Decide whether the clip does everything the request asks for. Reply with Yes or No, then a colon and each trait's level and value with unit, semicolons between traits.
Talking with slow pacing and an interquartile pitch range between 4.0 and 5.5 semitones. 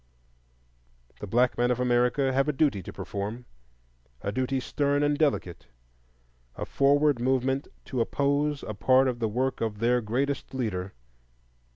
No: average, 145 wpm; average, 4.7 semitones